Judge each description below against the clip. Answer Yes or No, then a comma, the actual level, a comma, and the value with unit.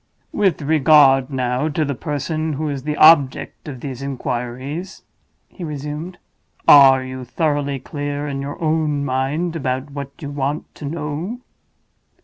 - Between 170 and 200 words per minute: No, average, 140 wpm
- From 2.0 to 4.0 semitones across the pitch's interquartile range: Yes, narrow, 2.6 semitones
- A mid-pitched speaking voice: Yes, medium, 145 Hz